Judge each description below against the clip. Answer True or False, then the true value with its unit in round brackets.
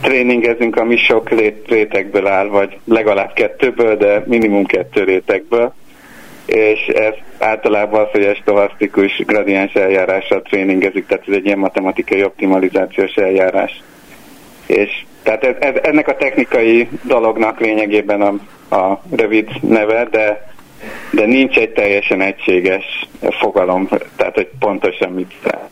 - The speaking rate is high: False (125 wpm)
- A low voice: True (105 Hz)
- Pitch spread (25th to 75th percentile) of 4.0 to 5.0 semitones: False (2.7 semitones)